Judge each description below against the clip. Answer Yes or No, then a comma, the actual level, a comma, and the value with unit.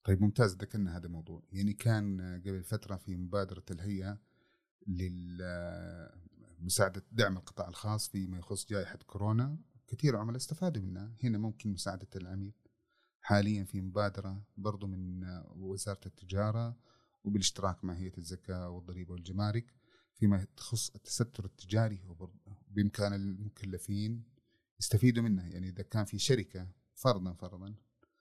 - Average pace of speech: No, slow, 120 wpm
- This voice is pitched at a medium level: No, low, 100 Hz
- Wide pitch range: No, average, 2.7 semitones